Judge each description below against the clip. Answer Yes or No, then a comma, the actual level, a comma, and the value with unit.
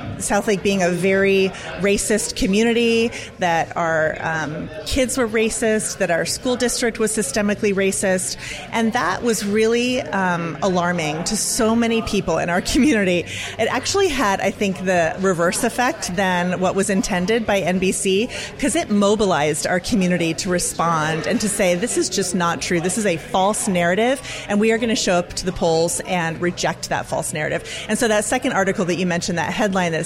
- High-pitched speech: Yes, high, 195 Hz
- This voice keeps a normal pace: Yes, average, 185 wpm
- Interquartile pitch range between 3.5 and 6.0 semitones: Yes, average, 4.1 semitones